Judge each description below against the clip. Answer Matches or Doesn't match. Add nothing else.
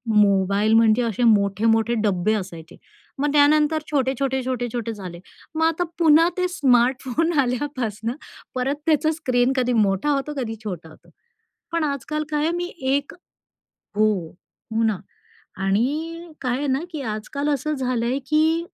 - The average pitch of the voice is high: Matches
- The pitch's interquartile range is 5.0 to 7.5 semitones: Matches